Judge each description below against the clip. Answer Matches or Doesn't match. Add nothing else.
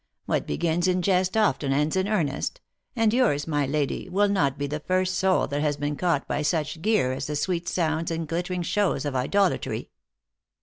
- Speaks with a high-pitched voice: Doesn't match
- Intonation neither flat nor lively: Matches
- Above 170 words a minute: Matches